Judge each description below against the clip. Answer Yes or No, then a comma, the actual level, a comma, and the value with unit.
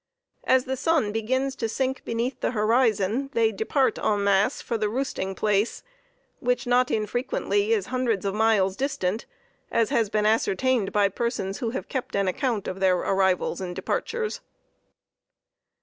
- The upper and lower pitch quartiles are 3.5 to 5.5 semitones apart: Yes, average, 4.4 semitones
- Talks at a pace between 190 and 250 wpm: No, average, 155 wpm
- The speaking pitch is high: Yes, high, 225 Hz